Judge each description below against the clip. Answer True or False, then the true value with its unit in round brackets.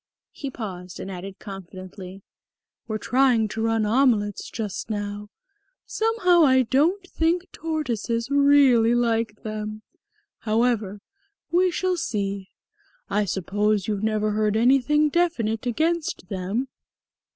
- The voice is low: False (225 Hz)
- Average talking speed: False (110 wpm)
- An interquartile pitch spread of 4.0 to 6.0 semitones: True (5.2 semitones)